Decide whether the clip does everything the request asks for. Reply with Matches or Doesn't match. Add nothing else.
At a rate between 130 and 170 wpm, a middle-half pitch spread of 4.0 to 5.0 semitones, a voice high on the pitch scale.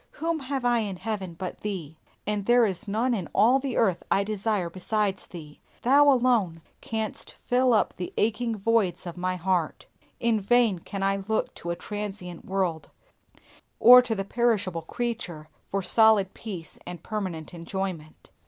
Matches